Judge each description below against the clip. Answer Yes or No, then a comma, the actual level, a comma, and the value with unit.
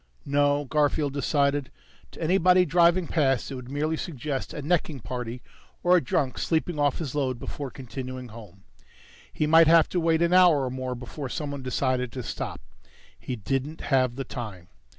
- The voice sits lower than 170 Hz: Yes, medium, 140 Hz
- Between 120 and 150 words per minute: No, average, 170 wpm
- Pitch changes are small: No, average, 3.8 semitones